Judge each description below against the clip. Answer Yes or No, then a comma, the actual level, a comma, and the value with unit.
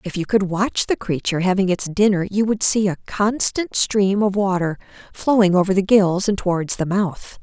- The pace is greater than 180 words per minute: Yes, average, 200 wpm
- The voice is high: Yes, high, 195 Hz